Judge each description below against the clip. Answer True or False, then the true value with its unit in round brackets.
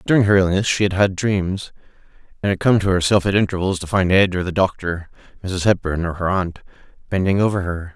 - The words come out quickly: True (210 wpm)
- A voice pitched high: False (95 Hz)